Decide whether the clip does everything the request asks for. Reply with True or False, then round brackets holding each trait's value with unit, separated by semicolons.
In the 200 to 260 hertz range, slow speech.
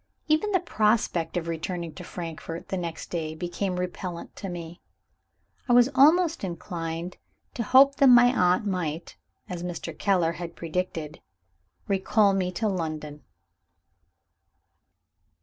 False (180 Hz; 130 wpm)